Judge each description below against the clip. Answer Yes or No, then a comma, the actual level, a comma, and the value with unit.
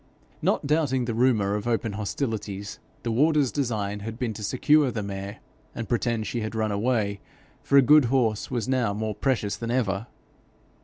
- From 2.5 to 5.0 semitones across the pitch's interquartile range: Yes, average, 3.7 semitones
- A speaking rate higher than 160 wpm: Yes, average, 175 wpm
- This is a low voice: Yes, low, 115 Hz